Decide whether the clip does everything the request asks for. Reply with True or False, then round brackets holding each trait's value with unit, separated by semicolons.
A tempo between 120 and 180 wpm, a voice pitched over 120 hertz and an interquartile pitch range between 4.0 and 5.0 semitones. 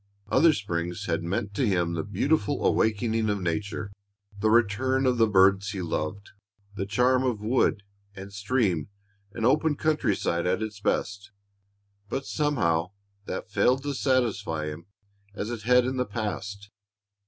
False (155 wpm; 105 Hz; 4.5 semitones)